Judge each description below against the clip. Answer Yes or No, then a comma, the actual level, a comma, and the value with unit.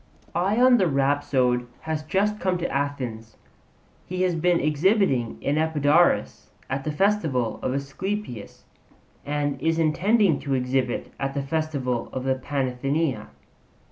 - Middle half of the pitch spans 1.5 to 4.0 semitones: No, average, 4.8 semitones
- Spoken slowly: Yes, slow, 130 wpm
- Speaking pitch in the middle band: Yes, medium, 145 Hz